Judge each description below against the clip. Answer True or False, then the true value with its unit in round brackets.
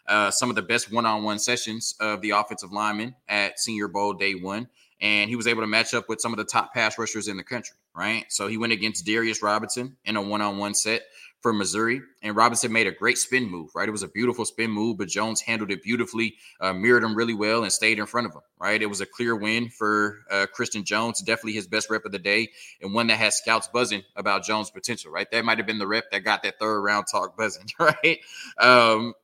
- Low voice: True (110 Hz)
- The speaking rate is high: True (240 wpm)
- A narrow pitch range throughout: True (1.8 semitones)